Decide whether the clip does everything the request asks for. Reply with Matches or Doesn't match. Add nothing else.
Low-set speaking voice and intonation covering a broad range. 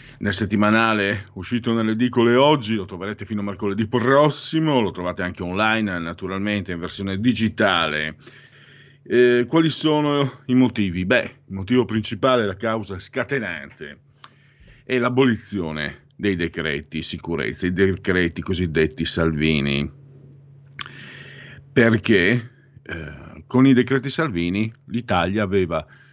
Matches